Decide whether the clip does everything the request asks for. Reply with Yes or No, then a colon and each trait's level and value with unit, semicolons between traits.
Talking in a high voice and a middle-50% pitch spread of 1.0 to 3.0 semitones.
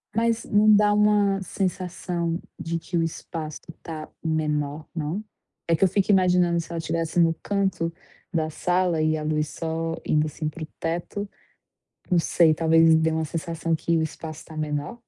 No: medium, 165 Hz; narrow, 2.4 semitones